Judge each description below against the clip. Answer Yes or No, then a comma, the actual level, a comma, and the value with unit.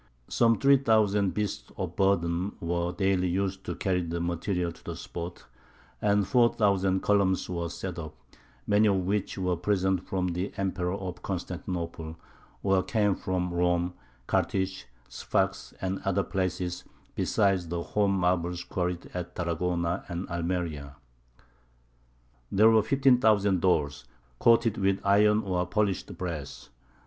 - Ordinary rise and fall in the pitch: No, narrow, 2.3 semitones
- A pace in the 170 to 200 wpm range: No, slow, 135 wpm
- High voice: No, very low, 95 Hz